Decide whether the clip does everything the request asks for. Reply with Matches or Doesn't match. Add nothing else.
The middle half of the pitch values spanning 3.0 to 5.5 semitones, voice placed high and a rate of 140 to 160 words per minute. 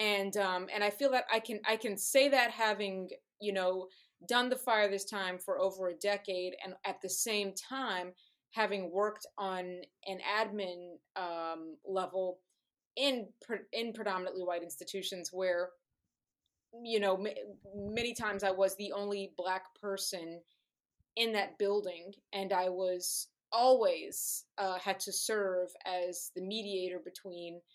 Doesn't match